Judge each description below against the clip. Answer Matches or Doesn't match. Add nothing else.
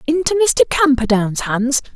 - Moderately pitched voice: Doesn't match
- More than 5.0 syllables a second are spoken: Doesn't match